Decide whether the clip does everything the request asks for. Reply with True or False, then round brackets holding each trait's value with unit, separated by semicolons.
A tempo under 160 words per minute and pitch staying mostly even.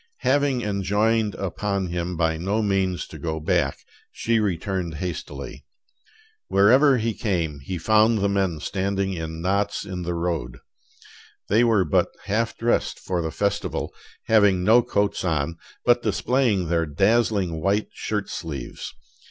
False (140 wpm; 4.1 semitones)